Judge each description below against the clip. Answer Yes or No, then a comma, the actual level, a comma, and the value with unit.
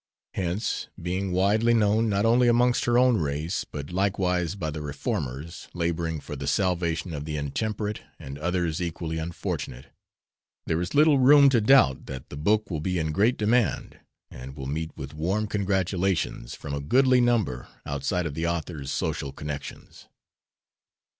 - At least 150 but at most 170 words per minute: Yes, average, 160 wpm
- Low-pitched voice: Yes, very low, 90 Hz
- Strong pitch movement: Yes, wide, 6.0 semitones